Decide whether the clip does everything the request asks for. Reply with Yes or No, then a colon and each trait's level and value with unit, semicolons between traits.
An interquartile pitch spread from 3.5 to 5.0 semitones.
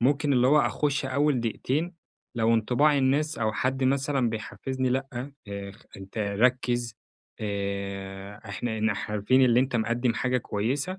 Yes: average, 3.8 semitones